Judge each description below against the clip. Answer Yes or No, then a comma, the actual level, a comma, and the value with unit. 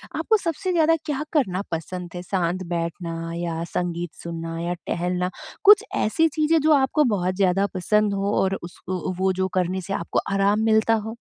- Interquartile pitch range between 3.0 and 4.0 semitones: No, average, 4.4 semitones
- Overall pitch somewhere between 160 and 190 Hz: Yes, medium, 185 Hz